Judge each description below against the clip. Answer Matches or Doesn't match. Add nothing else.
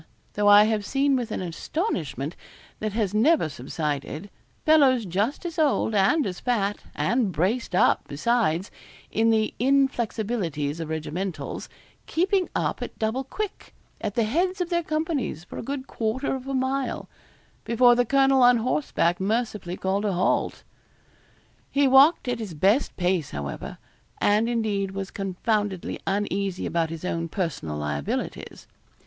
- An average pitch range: Doesn't match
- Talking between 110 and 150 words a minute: Matches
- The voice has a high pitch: Matches